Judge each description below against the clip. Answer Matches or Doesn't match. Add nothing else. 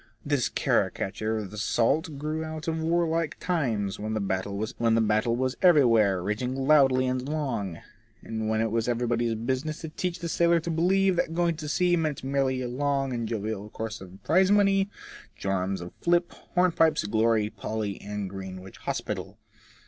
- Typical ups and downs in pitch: Doesn't match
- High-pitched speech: Doesn't match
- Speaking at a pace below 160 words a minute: Doesn't match